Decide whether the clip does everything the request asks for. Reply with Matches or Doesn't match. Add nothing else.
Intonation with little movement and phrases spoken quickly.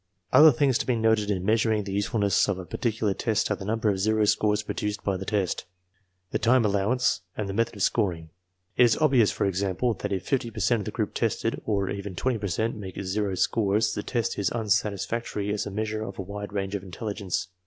Matches